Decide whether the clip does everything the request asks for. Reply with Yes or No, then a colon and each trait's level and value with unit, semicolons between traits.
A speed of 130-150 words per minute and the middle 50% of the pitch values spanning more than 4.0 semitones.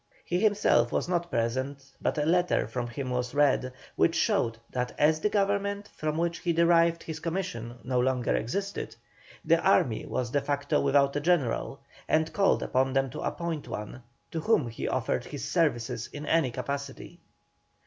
No: average, 170 wpm; average, 5.2 semitones